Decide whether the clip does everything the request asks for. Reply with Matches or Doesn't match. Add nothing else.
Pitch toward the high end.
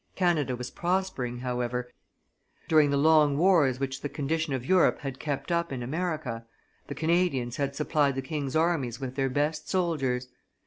Doesn't match